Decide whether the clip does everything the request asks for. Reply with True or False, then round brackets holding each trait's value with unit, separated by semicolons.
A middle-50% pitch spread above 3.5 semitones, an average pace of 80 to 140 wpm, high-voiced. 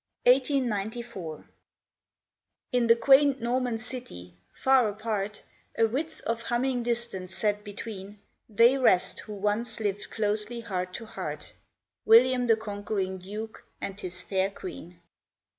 False (3.2 semitones; 135 wpm; 220 Hz)